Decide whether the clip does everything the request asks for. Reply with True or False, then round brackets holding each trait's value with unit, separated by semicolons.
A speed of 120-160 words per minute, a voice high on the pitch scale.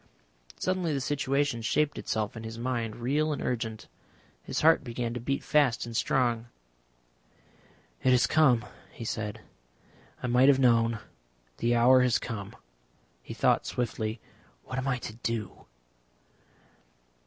False (140 wpm; 120 Hz)